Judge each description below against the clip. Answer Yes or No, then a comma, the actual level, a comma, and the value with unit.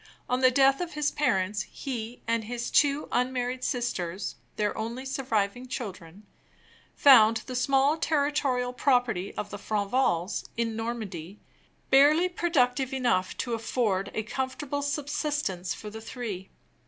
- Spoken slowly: Yes, slow, 130 wpm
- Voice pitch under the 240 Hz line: No, high, 245 Hz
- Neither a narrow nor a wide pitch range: Yes, average, 4.3 semitones